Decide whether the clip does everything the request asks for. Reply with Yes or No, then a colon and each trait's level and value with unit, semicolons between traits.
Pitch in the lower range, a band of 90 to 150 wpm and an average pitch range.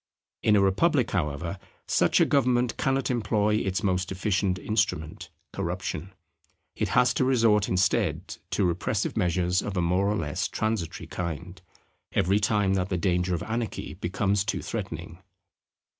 Yes: very low, 95 Hz; average, 145 wpm; average, 3.1 semitones